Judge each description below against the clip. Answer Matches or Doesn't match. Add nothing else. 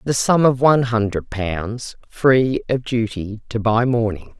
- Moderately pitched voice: Doesn't match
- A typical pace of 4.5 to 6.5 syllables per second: Doesn't match